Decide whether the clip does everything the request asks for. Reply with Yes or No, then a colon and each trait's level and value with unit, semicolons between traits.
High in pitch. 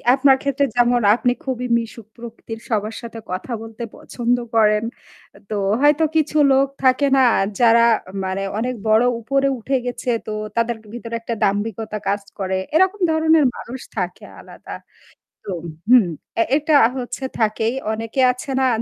Yes: high, 235 Hz